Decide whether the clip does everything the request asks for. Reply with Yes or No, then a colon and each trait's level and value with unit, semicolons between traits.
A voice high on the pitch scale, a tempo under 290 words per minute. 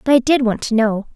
No: high, 240 Hz; fast, 310 wpm